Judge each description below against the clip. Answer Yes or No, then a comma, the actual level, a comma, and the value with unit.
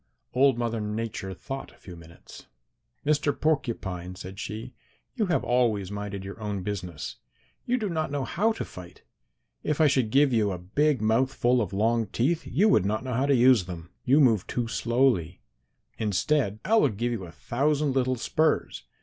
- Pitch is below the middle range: Yes, low, 120 Hz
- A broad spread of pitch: Yes, wide, 5.7 semitones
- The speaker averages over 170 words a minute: Yes, average, 185 wpm